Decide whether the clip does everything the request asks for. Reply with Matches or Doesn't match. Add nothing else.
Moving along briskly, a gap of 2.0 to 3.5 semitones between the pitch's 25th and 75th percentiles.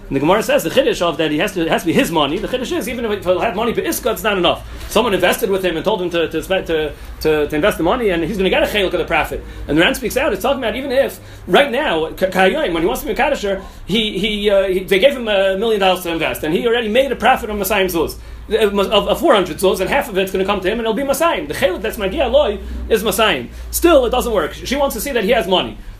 Doesn't match